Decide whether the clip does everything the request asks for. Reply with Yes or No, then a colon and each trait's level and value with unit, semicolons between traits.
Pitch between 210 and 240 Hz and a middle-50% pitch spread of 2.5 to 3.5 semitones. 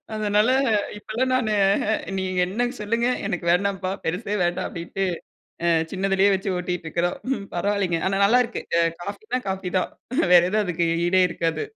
No: high, 195 Hz; average, 3.1 semitones